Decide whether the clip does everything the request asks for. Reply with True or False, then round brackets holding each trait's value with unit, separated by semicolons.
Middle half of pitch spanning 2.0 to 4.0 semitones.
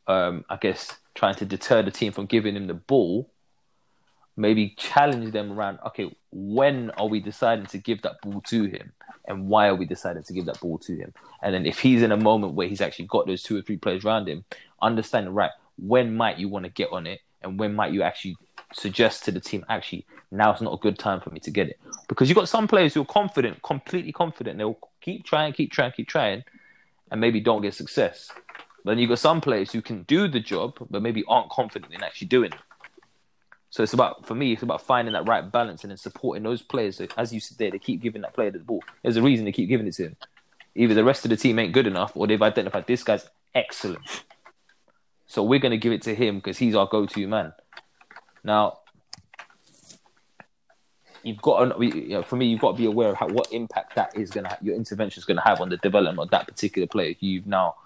True (3.0 semitones)